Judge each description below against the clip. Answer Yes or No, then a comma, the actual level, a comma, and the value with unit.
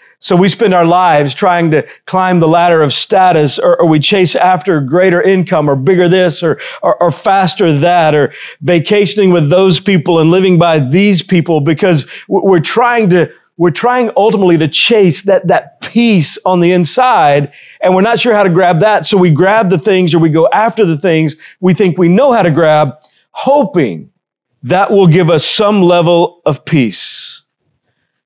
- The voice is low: No, medium, 180 Hz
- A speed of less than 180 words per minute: No, average, 185 wpm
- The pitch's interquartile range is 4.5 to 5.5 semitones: No, average, 3.1 semitones